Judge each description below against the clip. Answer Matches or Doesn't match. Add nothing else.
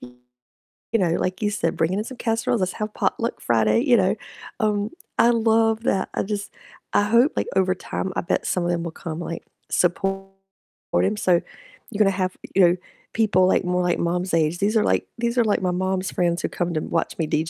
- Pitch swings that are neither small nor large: Matches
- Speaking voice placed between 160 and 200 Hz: Matches